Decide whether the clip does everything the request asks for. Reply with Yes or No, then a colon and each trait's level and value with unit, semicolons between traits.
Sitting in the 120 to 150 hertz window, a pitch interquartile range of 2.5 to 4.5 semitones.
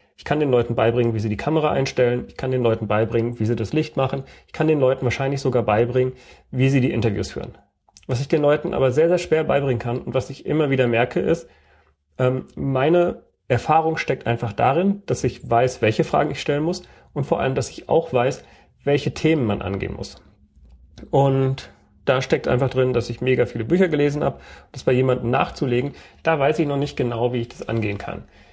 Yes: low, 130 Hz; average, 3.6 semitones